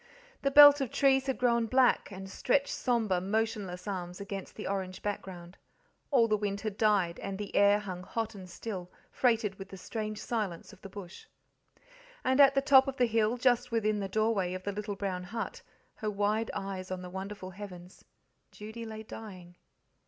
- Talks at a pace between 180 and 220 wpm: Yes, average, 185 wpm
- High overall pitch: Yes, high, 210 Hz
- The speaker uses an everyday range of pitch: Yes, average, 3.3 semitones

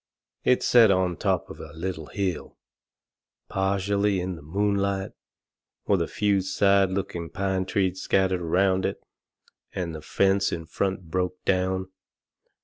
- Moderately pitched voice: No, very low, 95 Hz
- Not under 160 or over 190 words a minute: No, average, 140 wpm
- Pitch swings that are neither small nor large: No, narrow, 1.4 semitones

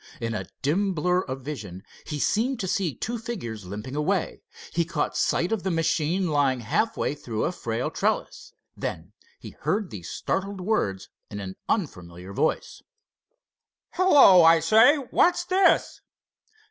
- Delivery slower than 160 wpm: Yes, average, 150 wpm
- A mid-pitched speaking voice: Yes, medium, 165 Hz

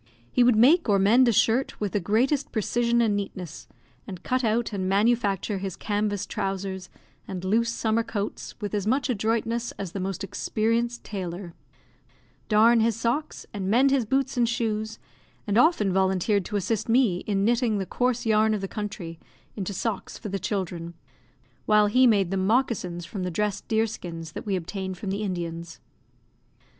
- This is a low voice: No, high, 210 Hz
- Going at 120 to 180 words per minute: Yes, average, 175 wpm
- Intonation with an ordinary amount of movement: Yes, average, 3.3 semitones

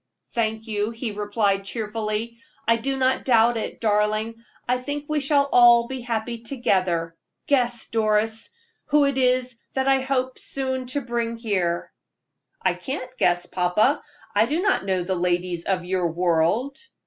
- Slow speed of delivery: No, average, 155 wpm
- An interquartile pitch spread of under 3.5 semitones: No, average, 4.0 semitones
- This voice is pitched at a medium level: No, high, 230 Hz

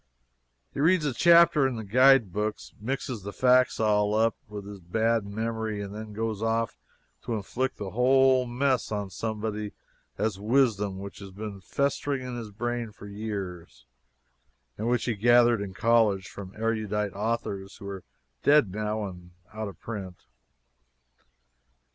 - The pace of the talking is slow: No, average, 150 wpm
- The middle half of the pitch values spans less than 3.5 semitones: Yes, average, 3.1 semitones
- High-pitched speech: No, low, 110 Hz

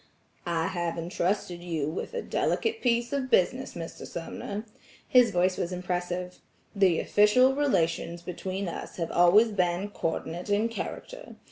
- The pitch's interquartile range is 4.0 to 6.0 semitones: Yes, average, 4.9 semitones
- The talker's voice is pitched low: No, medium, 185 Hz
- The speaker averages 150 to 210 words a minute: No, average, 140 wpm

